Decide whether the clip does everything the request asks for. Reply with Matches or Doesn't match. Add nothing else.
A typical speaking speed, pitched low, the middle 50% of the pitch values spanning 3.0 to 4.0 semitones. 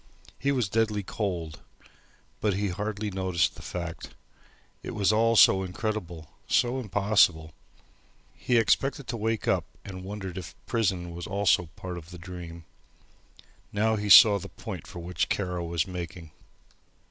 Matches